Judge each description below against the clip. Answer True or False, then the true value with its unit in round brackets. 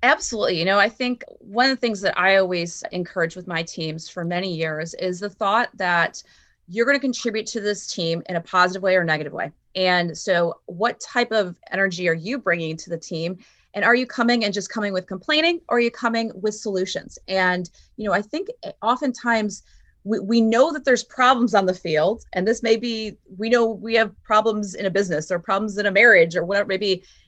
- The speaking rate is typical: False (220 wpm)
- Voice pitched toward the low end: False (200 Hz)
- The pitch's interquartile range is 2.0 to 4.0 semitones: False (4.4 semitones)